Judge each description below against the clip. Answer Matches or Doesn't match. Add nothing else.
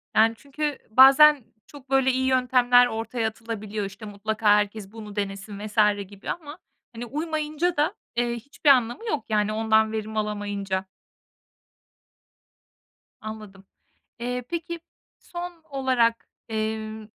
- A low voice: Doesn't match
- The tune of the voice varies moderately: Matches